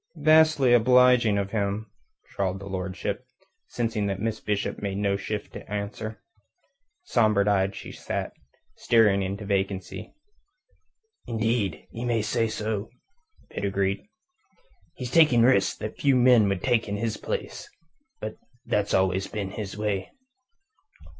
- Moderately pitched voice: No, low, 105 Hz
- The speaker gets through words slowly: Yes, slow, 130 wpm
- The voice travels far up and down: No, average, 2.8 semitones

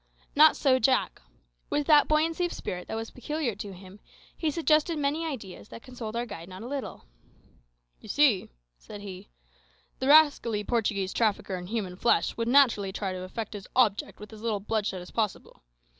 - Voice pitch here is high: Yes, high, 225 Hz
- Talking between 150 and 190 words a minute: Yes, average, 180 wpm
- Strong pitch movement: Yes, wide, 6.1 semitones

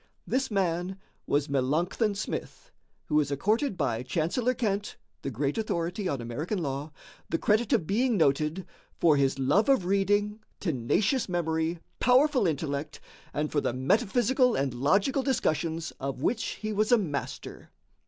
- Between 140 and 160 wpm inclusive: Yes, average, 145 wpm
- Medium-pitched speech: Yes, medium, 175 Hz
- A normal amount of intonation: No, wide, 7.0 semitones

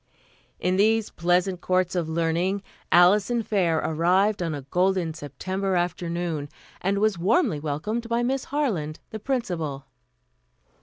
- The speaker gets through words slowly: Yes, slow, 125 wpm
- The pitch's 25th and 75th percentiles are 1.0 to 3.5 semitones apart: No, average, 4.0 semitones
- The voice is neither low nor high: Yes, medium, 180 Hz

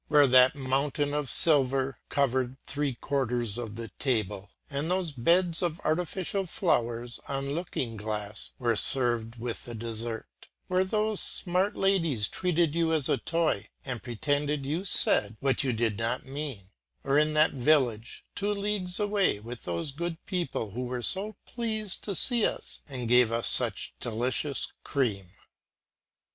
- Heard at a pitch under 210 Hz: Yes, low, 135 Hz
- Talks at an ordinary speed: Yes, average, 155 wpm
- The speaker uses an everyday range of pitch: No, wide, 6.1 semitones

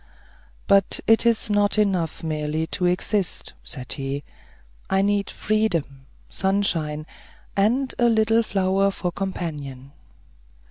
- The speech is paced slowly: Yes, slow, 120 wpm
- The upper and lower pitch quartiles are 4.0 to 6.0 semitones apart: Yes, average, 5.0 semitones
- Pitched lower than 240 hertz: Yes, high, 190 Hz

